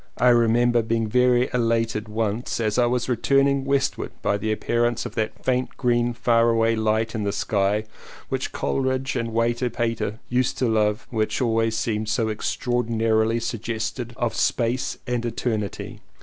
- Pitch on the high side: No, low, 115 Hz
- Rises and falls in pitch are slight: Yes, narrow, 1.8 semitones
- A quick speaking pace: No, average, 160 wpm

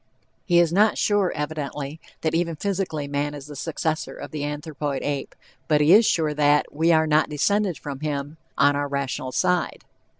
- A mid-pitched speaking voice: Yes, medium, 150 Hz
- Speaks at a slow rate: No, average, 175 wpm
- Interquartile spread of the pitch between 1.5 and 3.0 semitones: Yes, narrow, 2.4 semitones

